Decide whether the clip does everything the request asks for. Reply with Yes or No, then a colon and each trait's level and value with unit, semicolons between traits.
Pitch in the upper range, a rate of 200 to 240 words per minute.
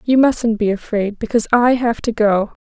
Yes: high, 225 Hz; fast, 205 wpm